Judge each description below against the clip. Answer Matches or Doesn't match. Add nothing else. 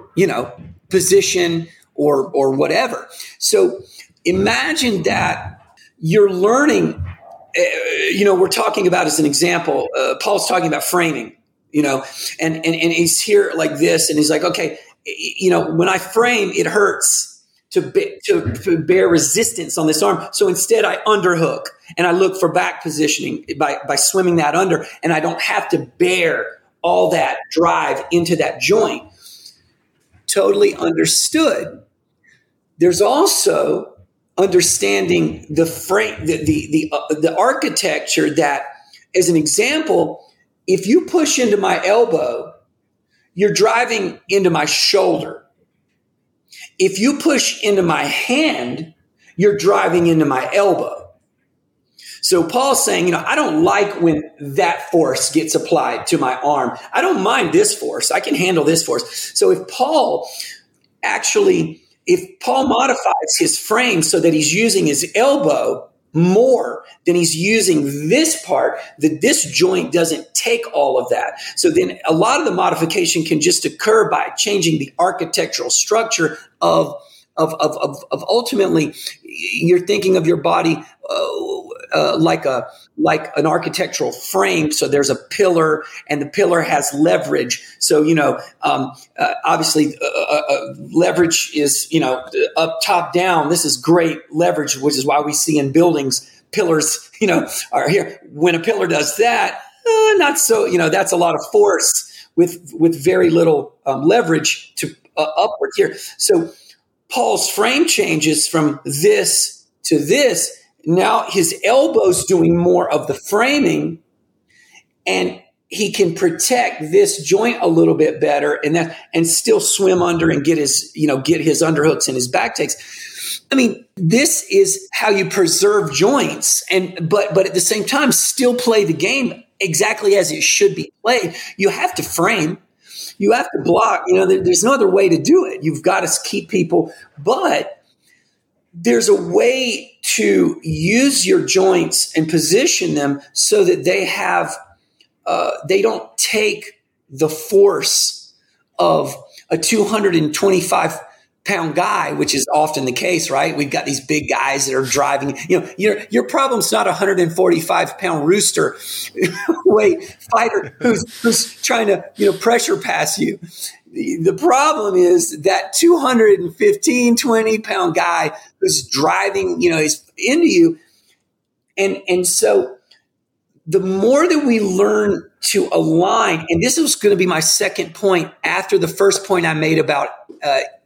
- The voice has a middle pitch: Doesn't match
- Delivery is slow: Doesn't match